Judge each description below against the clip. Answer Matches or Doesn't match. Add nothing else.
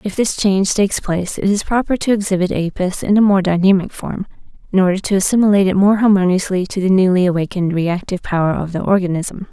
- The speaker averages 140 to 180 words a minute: Doesn't match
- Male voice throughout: Doesn't match